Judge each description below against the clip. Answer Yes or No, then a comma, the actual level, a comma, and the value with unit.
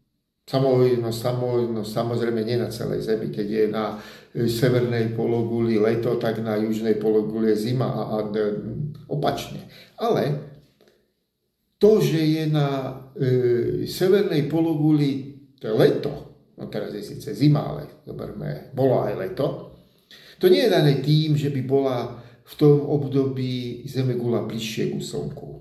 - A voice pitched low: Yes, low, 125 Hz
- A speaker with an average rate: Yes, average, 125 wpm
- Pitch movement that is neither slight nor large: Yes, average, 4.0 semitones